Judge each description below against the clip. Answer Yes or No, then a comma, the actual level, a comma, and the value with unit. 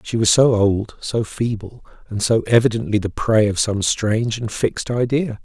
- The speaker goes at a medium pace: Yes, average, 190 wpm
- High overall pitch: No, low, 110 Hz